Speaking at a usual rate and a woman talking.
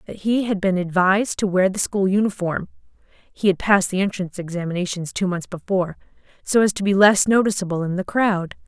Yes: average, 185 wpm; female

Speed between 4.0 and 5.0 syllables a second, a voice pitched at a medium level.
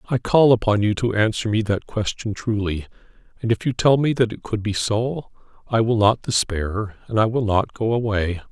No: 4.9 syllables/s; low, 110 Hz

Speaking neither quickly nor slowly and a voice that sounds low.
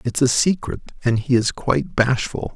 Yes: average, 190 wpm; low, 125 Hz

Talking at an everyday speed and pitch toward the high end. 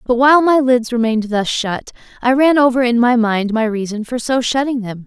No: fast, 225 wpm; high, 240 Hz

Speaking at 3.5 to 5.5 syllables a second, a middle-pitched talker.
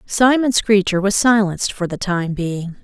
No: 4.5 syllables/s; high, 200 Hz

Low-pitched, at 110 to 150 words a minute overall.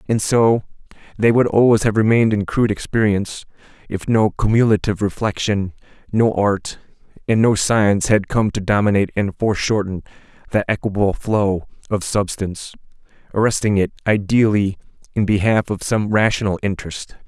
Yes: low, 105 Hz; slow, 135 wpm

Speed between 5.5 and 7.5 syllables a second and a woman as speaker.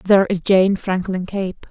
No: 4.4 syllables/s; female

